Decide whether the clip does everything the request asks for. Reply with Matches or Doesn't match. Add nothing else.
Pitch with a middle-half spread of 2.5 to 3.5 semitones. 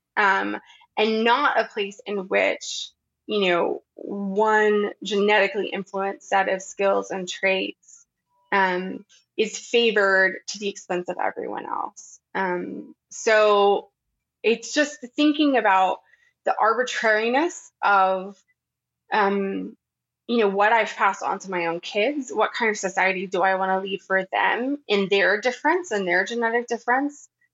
Doesn't match